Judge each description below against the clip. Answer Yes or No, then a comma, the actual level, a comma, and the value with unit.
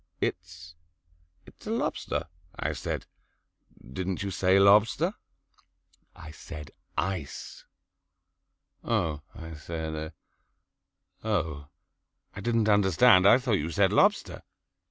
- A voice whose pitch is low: Yes, very low, 90 Hz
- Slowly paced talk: Yes, slow, 100 wpm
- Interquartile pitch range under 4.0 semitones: No, average, 4.3 semitones